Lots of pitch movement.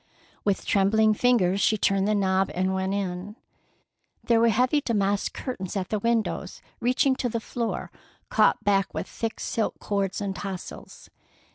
No: average, 2.9 semitones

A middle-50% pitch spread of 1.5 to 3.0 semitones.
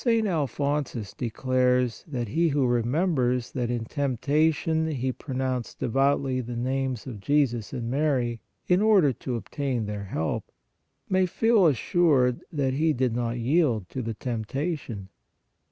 No: average, 3.9 semitones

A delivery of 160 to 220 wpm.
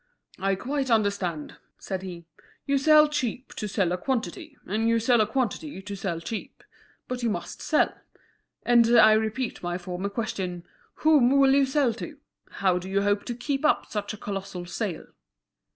Yes: average, 175 wpm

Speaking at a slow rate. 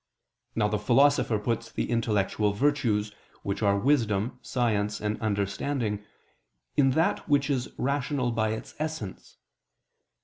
Yes: slow, 125 wpm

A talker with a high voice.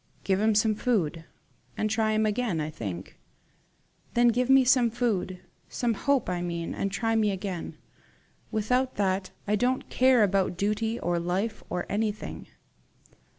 Yes: high, 215 Hz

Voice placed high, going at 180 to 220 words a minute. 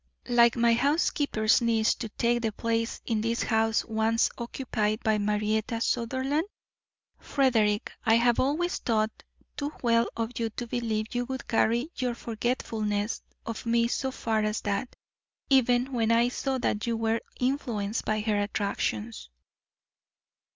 No: high, 230 Hz; average, 145 wpm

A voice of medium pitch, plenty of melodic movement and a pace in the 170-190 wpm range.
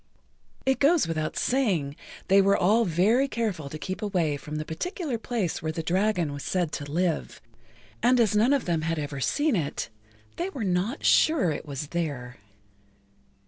Yes: medium, 180 Hz; wide, 7.0 semitones; average, 180 wpm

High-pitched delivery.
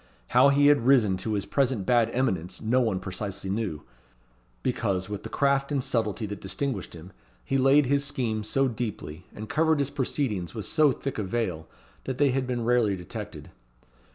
No: low, 115 Hz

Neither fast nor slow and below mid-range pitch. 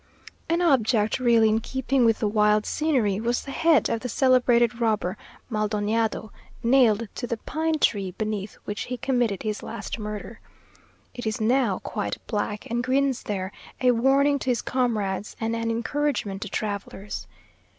No: average, 160 wpm; high, 230 Hz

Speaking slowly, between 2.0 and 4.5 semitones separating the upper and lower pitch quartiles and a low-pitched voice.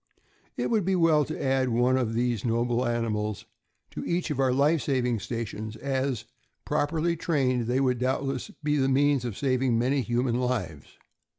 No: average, 170 wpm; average, 2.9 semitones; low, 130 Hz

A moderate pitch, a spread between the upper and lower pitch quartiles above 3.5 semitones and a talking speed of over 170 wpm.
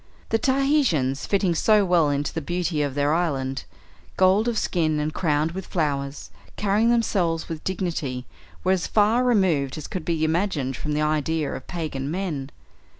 No: medium, 165 Hz; average, 4.6 semitones; average, 165 wpm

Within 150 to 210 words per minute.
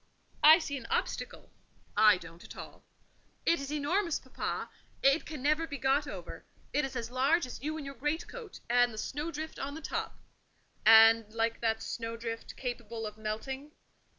Yes: average, 170 wpm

